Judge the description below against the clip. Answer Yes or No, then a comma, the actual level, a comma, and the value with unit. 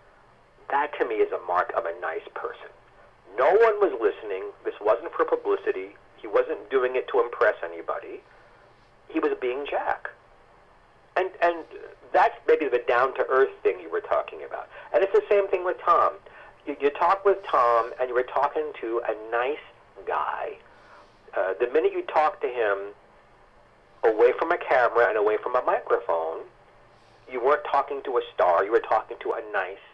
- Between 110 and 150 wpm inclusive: No, average, 175 wpm